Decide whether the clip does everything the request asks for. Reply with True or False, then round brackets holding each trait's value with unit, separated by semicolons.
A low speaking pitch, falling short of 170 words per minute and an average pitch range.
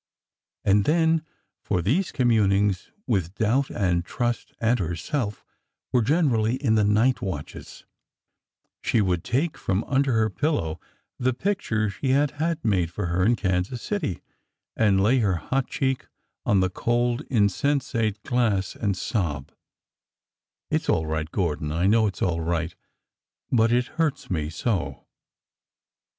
False (110 Hz; 145 wpm; 5.7 semitones)